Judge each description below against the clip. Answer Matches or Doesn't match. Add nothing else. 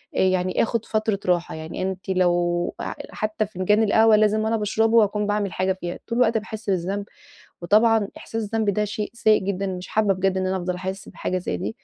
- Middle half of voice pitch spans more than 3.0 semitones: Doesn't match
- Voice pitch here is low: Doesn't match